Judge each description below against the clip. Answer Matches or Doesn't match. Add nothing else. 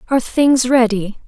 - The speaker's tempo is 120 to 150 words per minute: Matches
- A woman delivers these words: Matches